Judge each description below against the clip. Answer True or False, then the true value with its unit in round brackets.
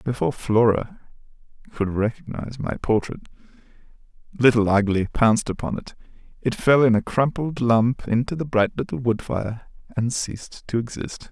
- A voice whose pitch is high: False (120 Hz)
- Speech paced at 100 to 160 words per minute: True (145 wpm)